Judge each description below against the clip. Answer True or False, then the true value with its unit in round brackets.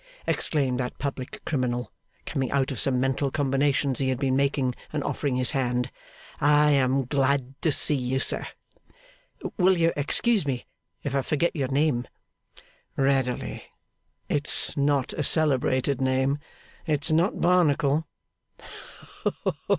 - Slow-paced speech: True (130 wpm)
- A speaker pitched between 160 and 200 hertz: False (140 Hz)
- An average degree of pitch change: False (2.1 semitones)